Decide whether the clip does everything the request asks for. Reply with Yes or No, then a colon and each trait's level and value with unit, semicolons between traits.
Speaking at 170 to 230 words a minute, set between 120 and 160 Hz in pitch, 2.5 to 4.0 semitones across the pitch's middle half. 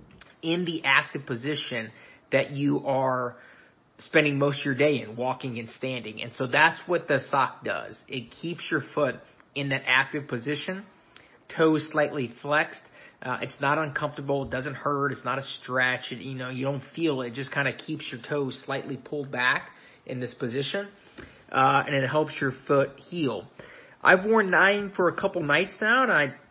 Yes: average, 185 wpm; medium, 140 Hz; average, 3.1 semitones